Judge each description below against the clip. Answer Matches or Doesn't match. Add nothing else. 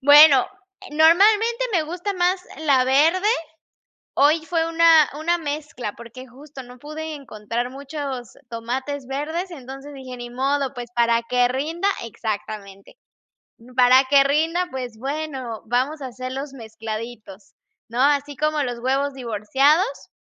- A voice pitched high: Matches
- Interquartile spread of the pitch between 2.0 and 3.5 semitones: Doesn't match